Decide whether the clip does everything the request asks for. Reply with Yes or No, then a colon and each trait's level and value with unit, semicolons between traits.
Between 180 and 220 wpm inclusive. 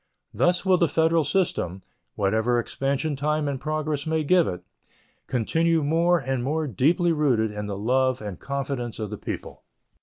No: average, 160 wpm